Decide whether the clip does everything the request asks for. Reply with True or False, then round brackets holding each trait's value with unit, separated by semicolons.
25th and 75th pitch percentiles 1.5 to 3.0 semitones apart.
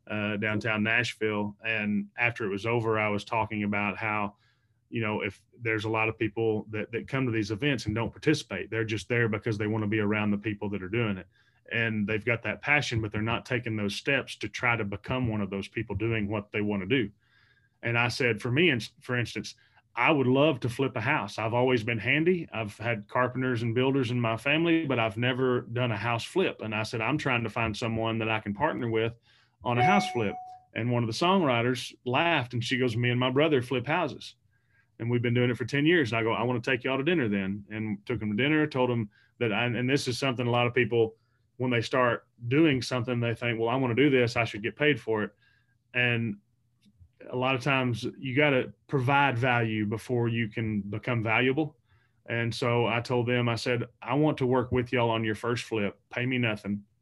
True (2.4 semitones)